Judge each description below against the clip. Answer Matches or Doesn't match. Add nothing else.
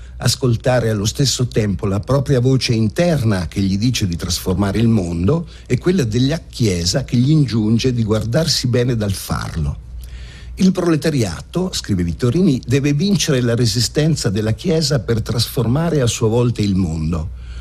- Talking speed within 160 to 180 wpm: Doesn't match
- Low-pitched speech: Matches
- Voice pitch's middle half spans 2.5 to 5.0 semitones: Doesn't match